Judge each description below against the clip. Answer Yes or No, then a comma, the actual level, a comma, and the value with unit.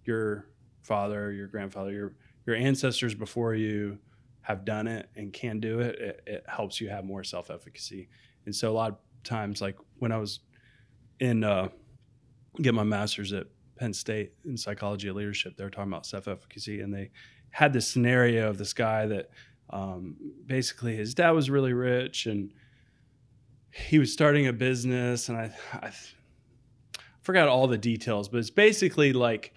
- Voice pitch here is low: Yes, low, 115 Hz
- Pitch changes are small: No, average, 3.4 semitones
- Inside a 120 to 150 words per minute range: No, average, 175 wpm